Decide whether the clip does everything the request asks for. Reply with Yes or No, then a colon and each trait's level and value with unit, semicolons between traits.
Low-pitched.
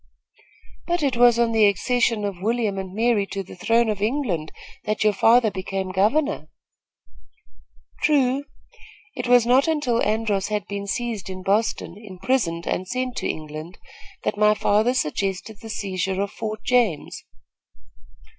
No: high, 215 Hz